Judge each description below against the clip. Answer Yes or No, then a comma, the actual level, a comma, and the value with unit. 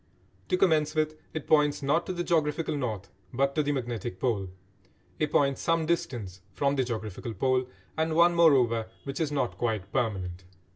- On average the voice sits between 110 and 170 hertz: Yes, medium, 140 Hz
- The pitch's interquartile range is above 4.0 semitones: Yes, average, 5.3 semitones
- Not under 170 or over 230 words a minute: Yes, average, 175 wpm